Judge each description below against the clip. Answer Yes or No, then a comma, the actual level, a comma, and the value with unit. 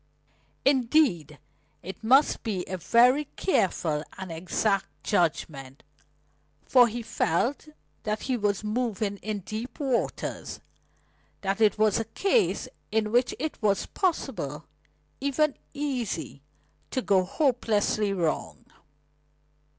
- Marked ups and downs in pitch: No, average, 5.0 semitones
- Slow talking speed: Yes, slow, 110 wpm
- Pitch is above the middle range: Yes, high, 215 Hz